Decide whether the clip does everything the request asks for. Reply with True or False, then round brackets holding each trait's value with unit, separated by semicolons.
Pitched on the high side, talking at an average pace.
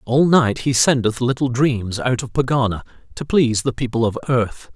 False (125 Hz; 190 wpm)